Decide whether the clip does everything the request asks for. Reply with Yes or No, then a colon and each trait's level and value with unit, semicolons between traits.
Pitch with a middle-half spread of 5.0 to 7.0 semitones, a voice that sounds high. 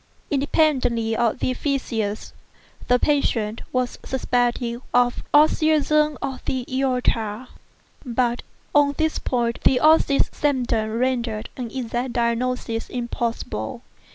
No: average, 2.8 semitones; very high, 250 Hz